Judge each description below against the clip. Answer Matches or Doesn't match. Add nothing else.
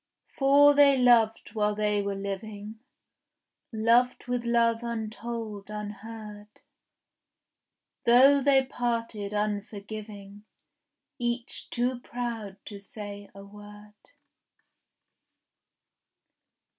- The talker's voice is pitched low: Doesn't match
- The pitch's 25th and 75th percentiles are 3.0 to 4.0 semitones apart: Doesn't match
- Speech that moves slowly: Matches